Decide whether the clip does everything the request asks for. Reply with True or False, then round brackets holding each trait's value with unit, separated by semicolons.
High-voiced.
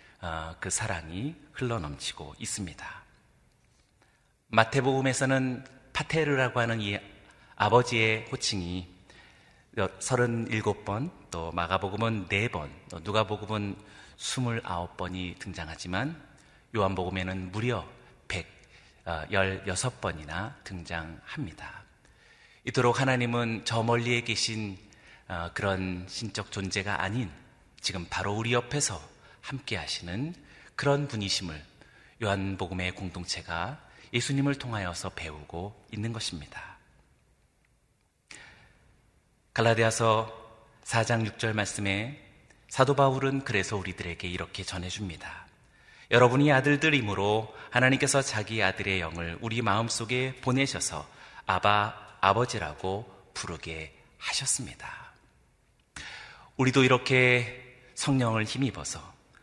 False (105 Hz)